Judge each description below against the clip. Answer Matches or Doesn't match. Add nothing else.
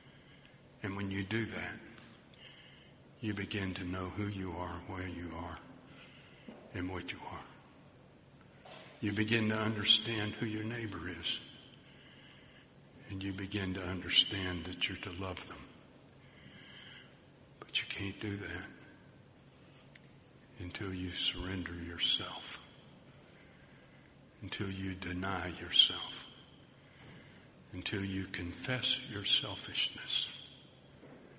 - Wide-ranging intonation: Doesn't match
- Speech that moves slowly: Matches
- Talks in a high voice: Doesn't match